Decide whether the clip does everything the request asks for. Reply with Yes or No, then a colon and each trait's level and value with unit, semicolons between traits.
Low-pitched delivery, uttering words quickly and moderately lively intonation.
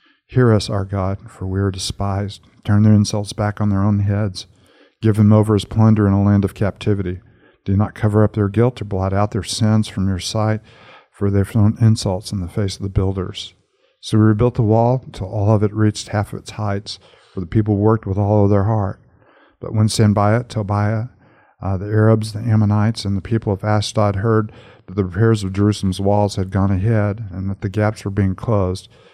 No: low, 105 Hz; fast, 215 wpm; narrow, 1.8 semitones